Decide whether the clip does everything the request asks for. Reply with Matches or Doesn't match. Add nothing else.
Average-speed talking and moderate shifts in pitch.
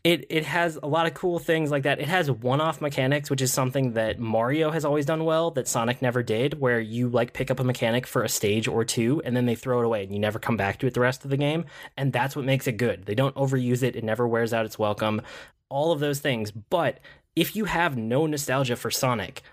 Doesn't match